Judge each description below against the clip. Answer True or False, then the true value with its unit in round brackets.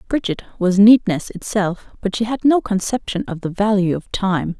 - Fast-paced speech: False (185 wpm)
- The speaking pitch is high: True (200 Hz)